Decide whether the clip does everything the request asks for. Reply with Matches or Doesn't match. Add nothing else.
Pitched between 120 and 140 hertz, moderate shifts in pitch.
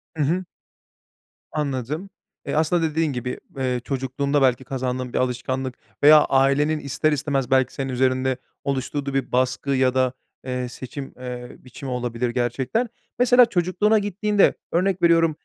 Matches